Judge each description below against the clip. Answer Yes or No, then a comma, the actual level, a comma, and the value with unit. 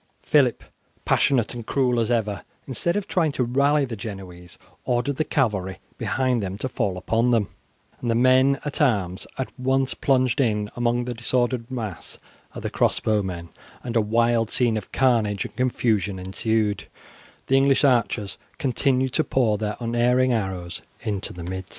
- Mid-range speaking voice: No, low, 120 Hz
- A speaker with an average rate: Yes, average, 165 wpm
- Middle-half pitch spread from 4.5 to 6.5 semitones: No, average, 3.8 semitones